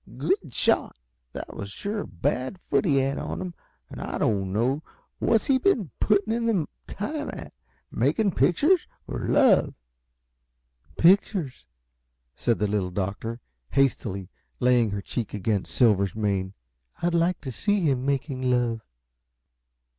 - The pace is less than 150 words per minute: Yes, average, 140 wpm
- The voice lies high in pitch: No, low, 135 Hz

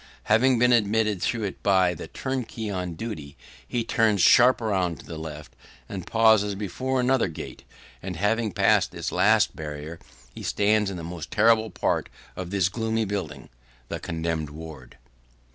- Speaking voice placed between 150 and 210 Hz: No, low, 100 Hz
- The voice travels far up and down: No, average, 4.8 semitones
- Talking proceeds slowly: No, average, 160 wpm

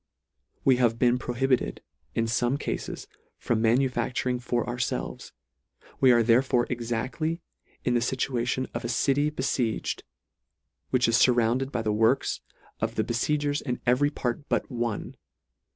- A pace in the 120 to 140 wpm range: Yes, slow, 135 wpm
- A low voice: Yes, low, 125 Hz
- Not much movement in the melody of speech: Yes, narrow, 2.0 semitones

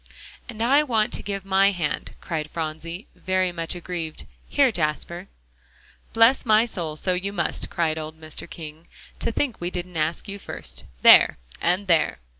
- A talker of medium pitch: Yes, medium, 180 Hz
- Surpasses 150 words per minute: Yes, average, 165 wpm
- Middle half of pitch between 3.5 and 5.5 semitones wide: Yes, average, 4.0 semitones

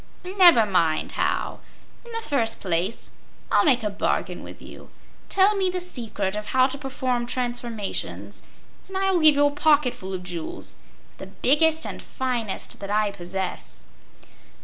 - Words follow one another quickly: No, average, 155 wpm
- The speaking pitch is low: No, high, 245 Hz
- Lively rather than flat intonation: Yes, wide, 7.6 semitones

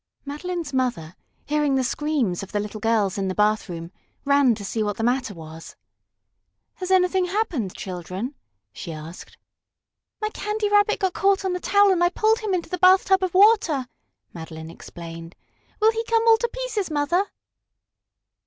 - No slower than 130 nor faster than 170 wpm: Yes, average, 165 wpm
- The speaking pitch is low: No, very high, 290 Hz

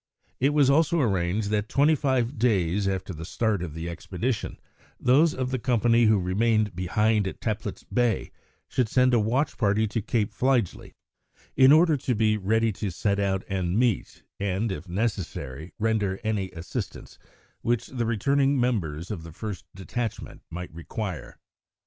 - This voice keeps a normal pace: Yes, average, 160 wpm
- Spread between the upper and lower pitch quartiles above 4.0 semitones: Yes, average, 4.5 semitones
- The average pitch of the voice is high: No, low, 110 Hz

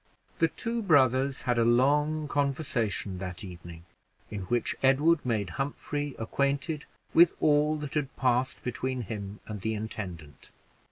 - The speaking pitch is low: Yes, low, 130 Hz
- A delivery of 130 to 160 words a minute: Yes, slow, 135 wpm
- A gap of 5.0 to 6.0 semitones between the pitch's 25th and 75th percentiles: Yes, wide, 5.6 semitones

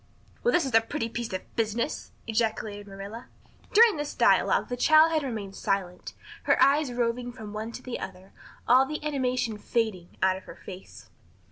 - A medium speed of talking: Yes, average, 175 wpm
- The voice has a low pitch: No, high, 230 Hz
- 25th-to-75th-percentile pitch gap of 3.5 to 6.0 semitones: Yes, average, 4.5 semitones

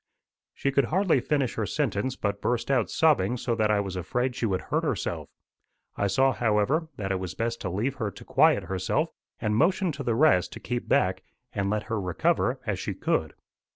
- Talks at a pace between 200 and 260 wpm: Yes, fast, 205 wpm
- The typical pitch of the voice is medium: No, low, 115 Hz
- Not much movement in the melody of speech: No, average, 5.2 semitones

